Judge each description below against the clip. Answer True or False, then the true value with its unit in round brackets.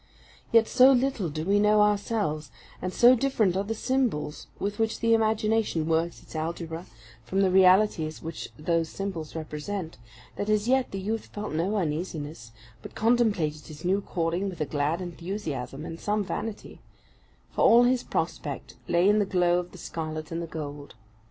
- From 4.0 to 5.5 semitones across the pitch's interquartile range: True (5.0 semitones)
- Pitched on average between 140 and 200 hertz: True (185 Hz)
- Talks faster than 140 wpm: True (170 wpm)